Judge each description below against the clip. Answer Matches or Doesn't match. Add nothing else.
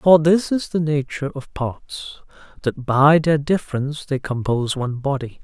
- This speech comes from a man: Matches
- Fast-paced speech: Doesn't match